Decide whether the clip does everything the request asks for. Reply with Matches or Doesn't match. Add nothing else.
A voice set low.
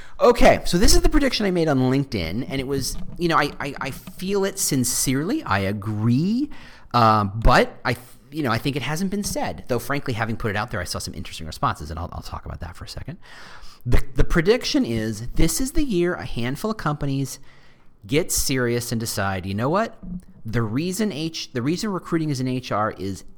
Matches